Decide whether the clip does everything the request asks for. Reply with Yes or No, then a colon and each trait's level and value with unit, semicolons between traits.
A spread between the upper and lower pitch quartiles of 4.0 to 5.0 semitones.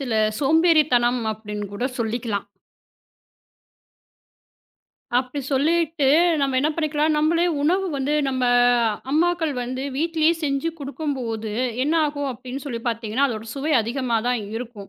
Yes: average, 4.3 semitones